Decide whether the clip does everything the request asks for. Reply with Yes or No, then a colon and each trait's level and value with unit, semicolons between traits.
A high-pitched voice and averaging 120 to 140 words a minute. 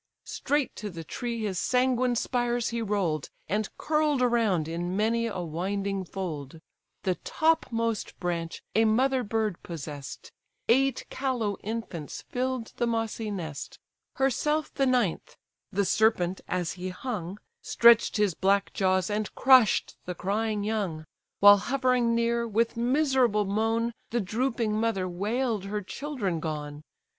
Yes: high, 215 Hz; slow, 135 wpm